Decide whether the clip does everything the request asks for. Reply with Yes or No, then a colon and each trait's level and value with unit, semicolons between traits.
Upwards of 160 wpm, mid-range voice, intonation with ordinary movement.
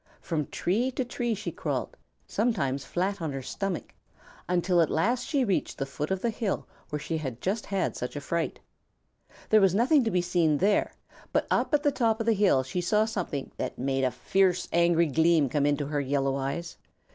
No: fast, 205 wpm; medium, 175 Hz; wide, 6.4 semitones